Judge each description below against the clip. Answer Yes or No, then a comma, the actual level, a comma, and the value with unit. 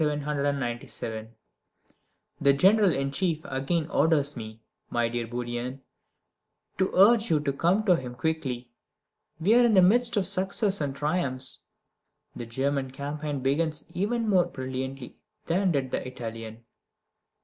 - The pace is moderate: No, slow, 130 wpm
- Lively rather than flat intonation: Yes, wide, 6.0 semitones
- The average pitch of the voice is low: No, medium, 145 Hz